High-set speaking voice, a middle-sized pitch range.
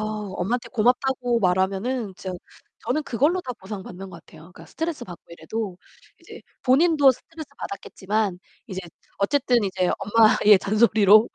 Yes: high, 215 Hz; average, 4.9 semitones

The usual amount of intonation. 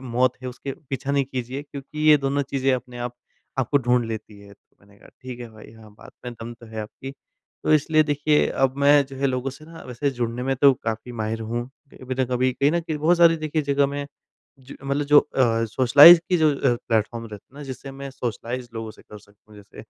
Yes: average, 3.3 semitones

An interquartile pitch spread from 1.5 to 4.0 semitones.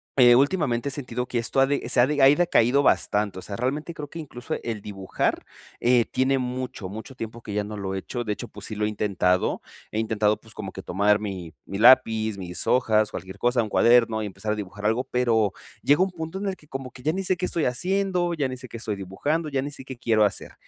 No: average, 4.5 semitones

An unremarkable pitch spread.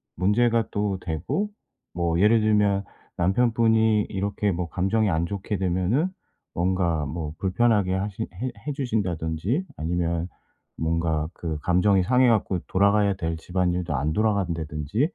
Yes: average, 4.1 semitones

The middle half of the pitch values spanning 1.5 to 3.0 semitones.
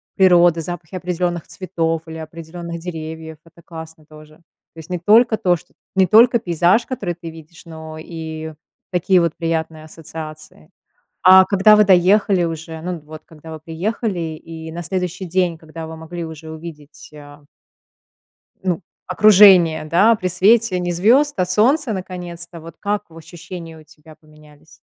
Yes: narrow, 2.6 semitones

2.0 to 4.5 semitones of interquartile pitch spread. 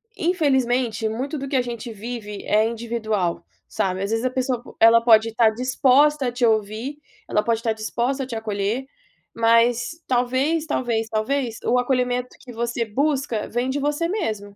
Yes: average, 3.0 semitones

